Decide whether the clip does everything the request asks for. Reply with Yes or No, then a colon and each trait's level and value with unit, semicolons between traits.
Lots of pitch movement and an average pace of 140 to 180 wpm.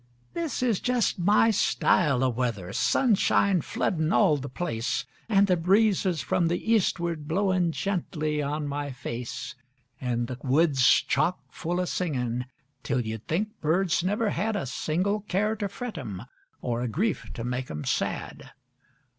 Yes: wide, 7.5 semitones; average, 155 wpm